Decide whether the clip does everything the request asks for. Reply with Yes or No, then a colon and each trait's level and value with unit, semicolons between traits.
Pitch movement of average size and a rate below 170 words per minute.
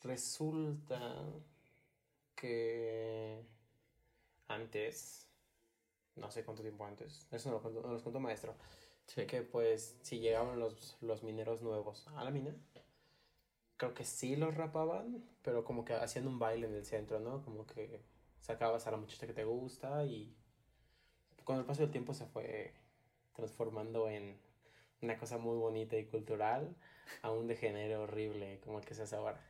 Yes: average, 3.0 semitones; average, 160 wpm